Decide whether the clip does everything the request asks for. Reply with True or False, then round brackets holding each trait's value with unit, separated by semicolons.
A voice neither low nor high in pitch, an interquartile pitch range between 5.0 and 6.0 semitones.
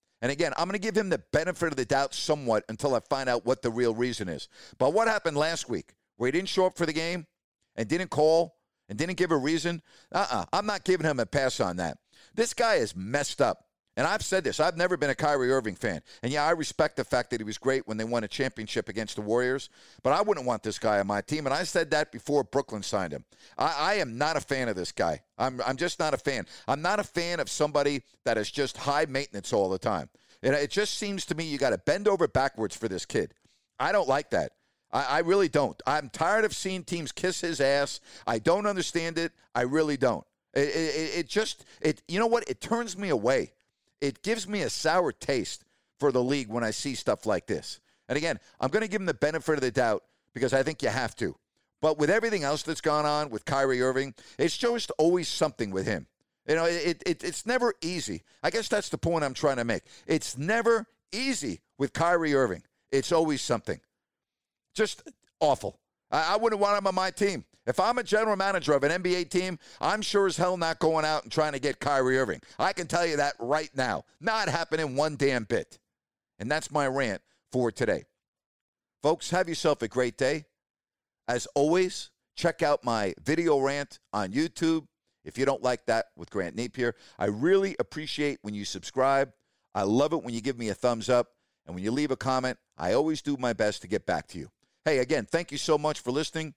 True (150 Hz; 5.4 semitones)